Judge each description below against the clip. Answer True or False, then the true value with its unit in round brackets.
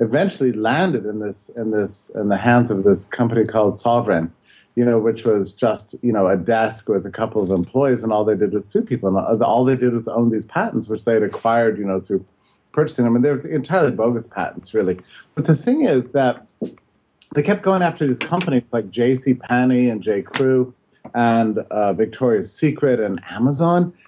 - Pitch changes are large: False (3.4 semitones)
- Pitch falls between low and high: False (120 Hz)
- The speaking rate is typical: False (210 wpm)